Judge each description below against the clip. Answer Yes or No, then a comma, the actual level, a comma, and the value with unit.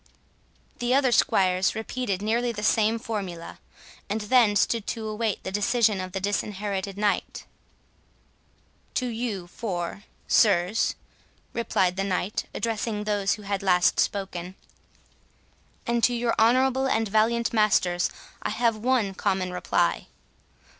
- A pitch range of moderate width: Yes, average, 3.2 semitones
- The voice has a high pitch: Yes, high, 210 Hz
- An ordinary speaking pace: No, slow, 125 wpm